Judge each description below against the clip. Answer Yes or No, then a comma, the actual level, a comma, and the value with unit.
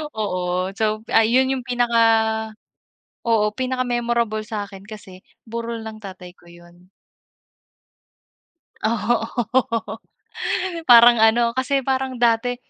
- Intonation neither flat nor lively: No, narrow, 2.2 semitones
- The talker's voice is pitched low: No, high, 230 Hz